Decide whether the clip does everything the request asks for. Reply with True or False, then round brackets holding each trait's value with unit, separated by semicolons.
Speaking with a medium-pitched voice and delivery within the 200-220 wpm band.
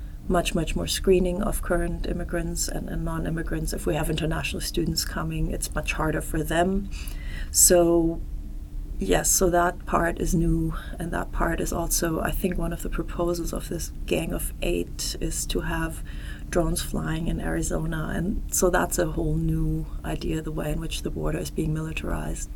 False (160 Hz; 180 wpm)